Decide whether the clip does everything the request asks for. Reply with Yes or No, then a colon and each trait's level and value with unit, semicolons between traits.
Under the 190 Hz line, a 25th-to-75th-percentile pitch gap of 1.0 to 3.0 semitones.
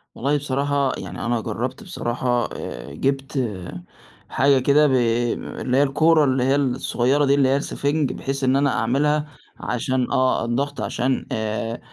Yes: low, 135 Hz; narrow, 2.6 semitones